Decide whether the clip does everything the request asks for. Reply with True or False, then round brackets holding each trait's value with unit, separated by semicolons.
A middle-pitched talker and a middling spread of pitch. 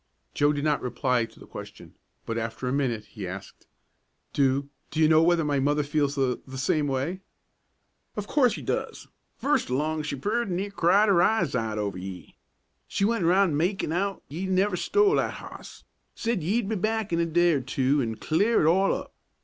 False (155 Hz; 6.5 semitones)